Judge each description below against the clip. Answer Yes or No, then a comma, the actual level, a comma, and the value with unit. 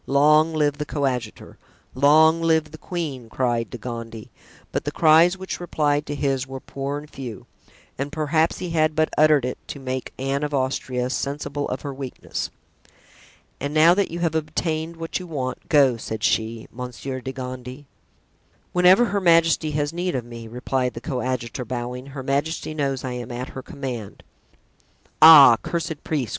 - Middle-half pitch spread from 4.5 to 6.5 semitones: No, average, 3.7 semitones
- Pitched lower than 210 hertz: Yes, medium, 140 Hz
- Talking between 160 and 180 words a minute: Yes, average, 170 wpm